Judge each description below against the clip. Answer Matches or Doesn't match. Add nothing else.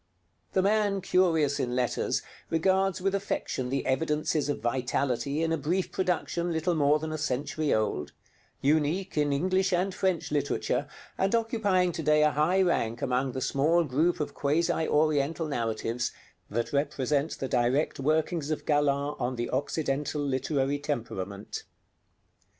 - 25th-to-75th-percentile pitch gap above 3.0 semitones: Matches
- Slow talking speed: Doesn't match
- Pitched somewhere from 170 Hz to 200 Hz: Doesn't match